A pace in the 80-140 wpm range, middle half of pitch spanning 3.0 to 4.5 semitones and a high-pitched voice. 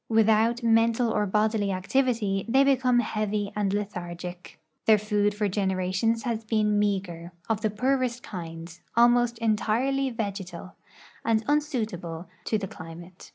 Yes: slow, 135 wpm; average, 3.4 semitones; high, 215 Hz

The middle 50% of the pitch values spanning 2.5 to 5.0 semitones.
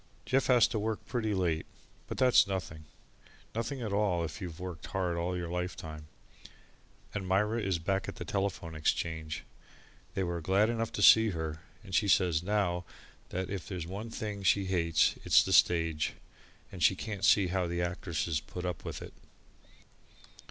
Yes: average, 3.4 semitones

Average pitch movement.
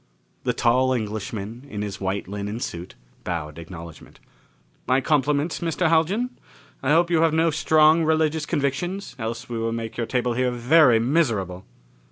No: wide, 6.9 semitones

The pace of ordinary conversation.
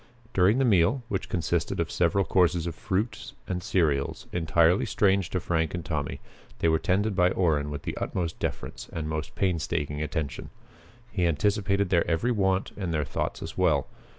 Yes: average, 175 wpm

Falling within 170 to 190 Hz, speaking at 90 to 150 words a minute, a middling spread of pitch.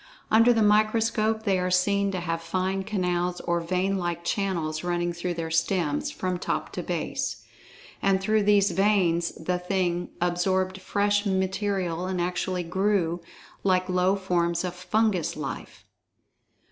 No: medium, 185 Hz; average, 145 wpm; narrow, 2.3 semitones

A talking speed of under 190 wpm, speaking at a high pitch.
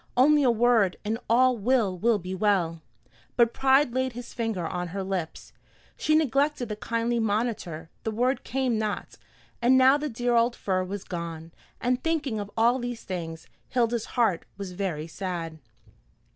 Yes: average, 160 wpm; high, 225 Hz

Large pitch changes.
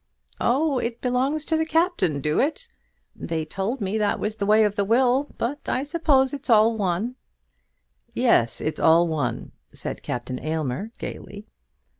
Yes: wide, 7.7 semitones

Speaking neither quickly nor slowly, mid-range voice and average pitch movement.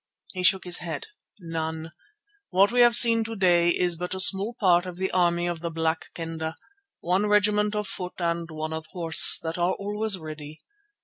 Yes: average, 190 wpm; medium, 175 Hz; average, 3.5 semitones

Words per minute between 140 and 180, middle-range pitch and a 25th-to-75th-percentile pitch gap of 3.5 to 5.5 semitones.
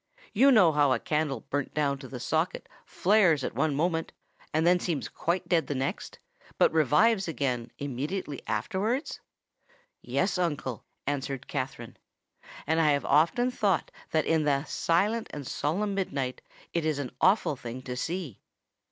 Yes: average, 155 wpm; medium, 155 Hz; average, 4.7 semitones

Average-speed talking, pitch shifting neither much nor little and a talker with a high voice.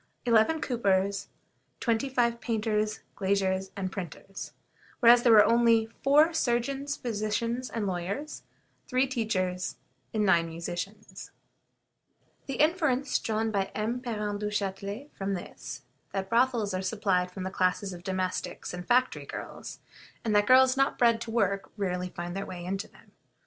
Yes: average, 145 wpm; average, 3.9 semitones; high, 210 Hz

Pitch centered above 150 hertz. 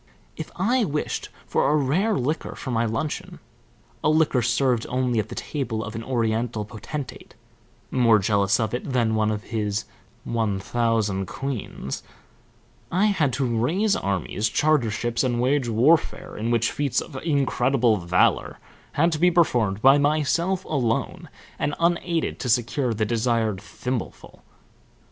No: low, 120 Hz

